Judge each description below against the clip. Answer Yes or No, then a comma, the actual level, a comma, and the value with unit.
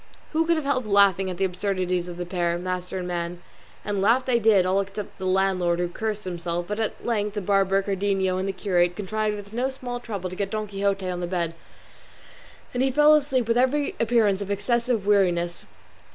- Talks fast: Yes, fast, 210 wpm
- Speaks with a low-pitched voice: No, high, 195 Hz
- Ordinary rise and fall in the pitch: Yes, average, 3.3 semitones